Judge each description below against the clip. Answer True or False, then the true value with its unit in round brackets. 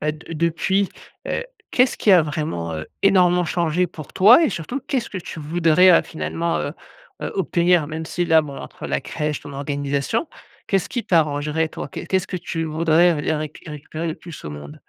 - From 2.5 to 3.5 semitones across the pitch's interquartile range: True (3.1 semitones)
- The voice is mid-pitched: True (160 Hz)